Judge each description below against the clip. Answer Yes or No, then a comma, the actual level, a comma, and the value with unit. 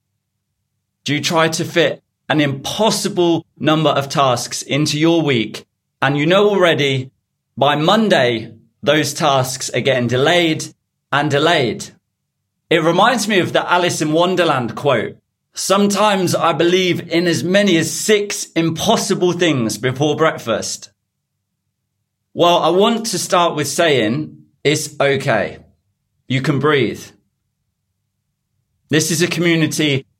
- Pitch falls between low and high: Yes, medium, 150 Hz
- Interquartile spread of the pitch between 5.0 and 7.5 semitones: Yes, average, 5.3 semitones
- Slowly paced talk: Yes, slow, 125 wpm